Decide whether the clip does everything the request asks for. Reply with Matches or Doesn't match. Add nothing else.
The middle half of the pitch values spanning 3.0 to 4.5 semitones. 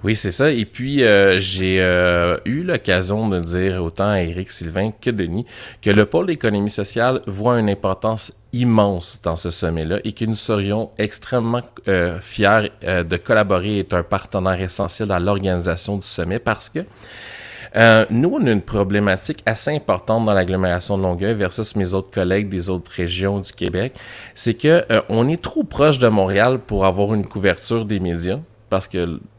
Matches